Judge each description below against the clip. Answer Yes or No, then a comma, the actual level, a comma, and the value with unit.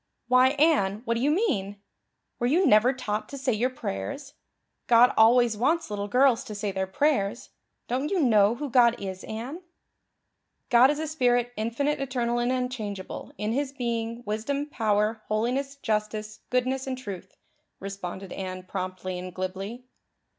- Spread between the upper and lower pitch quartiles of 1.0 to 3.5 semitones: No, average, 4.2 semitones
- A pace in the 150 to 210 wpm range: Yes, average, 155 wpm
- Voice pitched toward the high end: Yes, high, 235 Hz